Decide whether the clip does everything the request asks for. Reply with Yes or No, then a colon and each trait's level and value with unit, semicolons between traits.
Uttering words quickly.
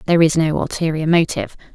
No: average, 170 wpm